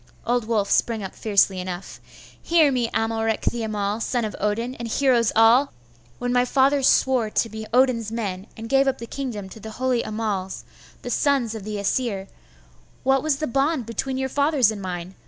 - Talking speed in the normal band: Yes, average, 190 wpm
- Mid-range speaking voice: No, high, 230 Hz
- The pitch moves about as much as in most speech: Yes, average, 3.7 semitones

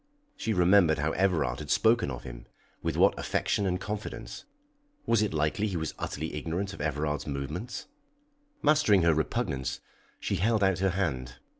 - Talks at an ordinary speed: Yes, average, 160 wpm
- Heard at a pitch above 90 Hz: No, very low, 85 Hz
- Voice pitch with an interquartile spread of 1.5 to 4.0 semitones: No, wide, 5.5 semitones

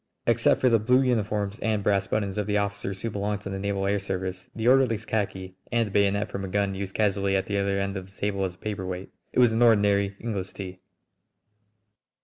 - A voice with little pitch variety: Yes, narrow, 1.6 semitones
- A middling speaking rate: No, fast, 220 wpm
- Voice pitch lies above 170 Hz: No, low, 100 Hz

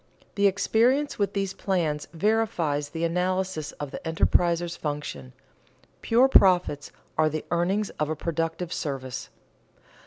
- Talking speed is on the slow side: Yes, slow, 125 wpm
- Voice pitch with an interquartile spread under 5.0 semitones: Yes, average, 4.3 semitones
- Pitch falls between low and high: Yes, medium, 170 Hz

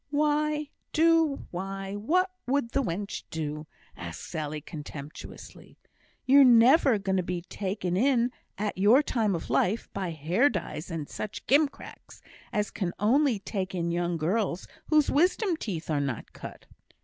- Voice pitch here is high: Yes, high, 200 Hz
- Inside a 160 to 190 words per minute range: No, average, 145 wpm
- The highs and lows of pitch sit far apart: Yes, wide, 7.3 semitones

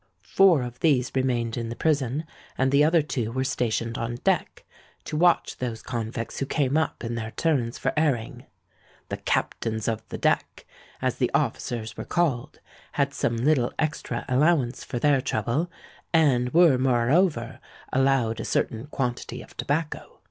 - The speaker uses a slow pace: No, average, 160 wpm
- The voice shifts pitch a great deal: No, average, 4.2 semitones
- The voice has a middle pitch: No, low, 130 Hz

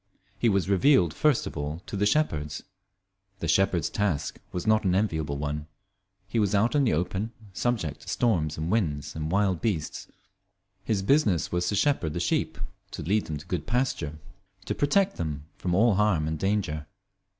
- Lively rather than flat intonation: Yes, wide, 5.7 semitones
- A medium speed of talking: Yes, average, 180 wpm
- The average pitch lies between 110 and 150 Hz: No, very low, 95 Hz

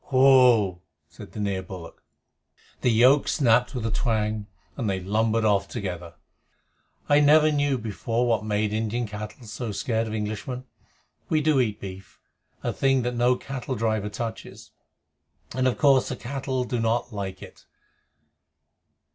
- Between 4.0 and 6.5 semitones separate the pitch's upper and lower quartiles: No, average, 3.5 semitones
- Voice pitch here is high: No, low, 115 Hz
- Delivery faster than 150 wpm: No, average, 145 wpm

